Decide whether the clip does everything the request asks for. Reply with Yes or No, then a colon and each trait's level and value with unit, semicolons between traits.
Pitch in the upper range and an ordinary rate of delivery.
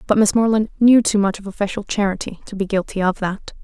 No: high, 205 Hz; fast, 230 wpm